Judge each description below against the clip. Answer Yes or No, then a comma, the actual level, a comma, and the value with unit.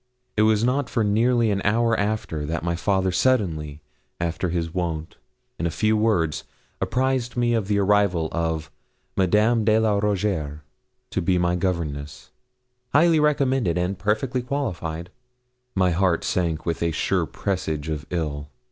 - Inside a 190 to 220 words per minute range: No, average, 150 wpm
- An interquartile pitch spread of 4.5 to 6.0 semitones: Yes, average, 5.0 semitones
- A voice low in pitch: Yes, very low, 95 Hz